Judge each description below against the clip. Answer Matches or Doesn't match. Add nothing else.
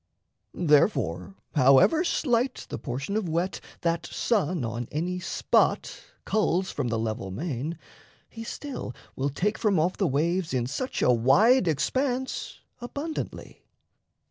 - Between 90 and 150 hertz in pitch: Doesn't match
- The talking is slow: Matches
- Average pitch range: Doesn't match